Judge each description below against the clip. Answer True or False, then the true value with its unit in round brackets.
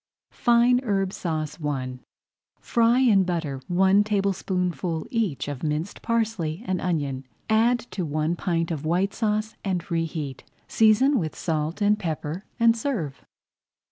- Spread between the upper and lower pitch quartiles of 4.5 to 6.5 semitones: True (5.5 semitones)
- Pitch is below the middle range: False (180 Hz)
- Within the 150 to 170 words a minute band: False (135 wpm)